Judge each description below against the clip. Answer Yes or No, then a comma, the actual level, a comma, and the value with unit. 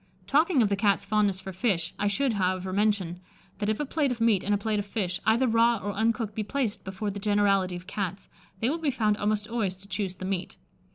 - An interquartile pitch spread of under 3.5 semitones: Yes, average, 3.0 semitones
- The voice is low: No, high, 205 Hz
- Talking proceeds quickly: Yes, fast, 235 wpm